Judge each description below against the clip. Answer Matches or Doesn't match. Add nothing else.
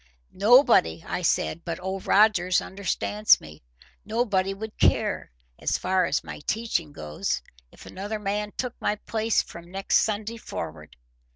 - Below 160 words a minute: Matches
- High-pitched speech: Matches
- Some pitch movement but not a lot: Matches